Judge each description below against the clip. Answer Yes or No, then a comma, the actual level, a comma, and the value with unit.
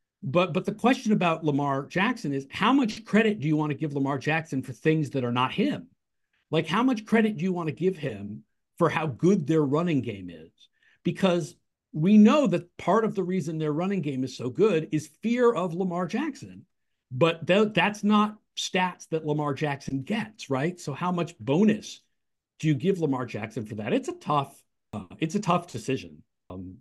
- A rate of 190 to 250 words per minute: Yes, average, 200 wpm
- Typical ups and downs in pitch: No, wide, 6.2 semitones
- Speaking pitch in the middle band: Yes, medium, 165 Hz